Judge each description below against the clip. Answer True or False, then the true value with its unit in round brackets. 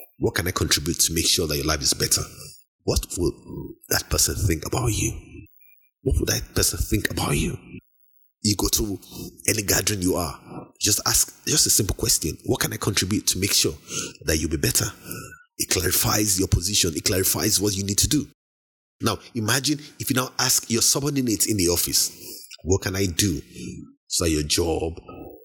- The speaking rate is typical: True (185 wpm)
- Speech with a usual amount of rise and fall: False (5.8 semitones)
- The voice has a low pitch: True (105 Hz)